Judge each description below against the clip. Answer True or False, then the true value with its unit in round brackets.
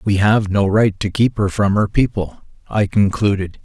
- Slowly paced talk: False (200 wpm)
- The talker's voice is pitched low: True (105 Hz)